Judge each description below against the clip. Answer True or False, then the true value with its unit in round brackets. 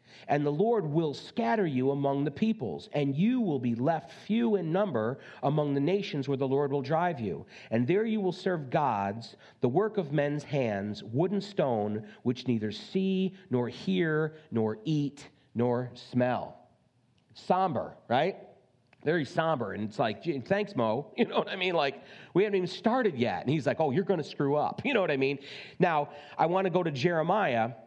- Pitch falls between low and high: True (150 Hz)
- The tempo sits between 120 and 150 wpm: False (190 wpm)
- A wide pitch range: True (6.7 semitones)